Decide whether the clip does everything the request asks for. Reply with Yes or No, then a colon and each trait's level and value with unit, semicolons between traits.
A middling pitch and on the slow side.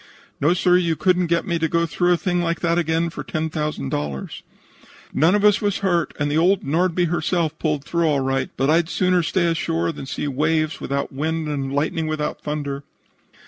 No: medium, 160 Hz; average, 185 wpm